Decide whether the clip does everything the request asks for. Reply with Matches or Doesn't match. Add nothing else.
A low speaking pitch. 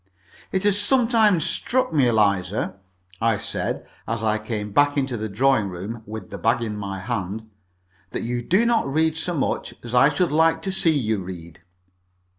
Matches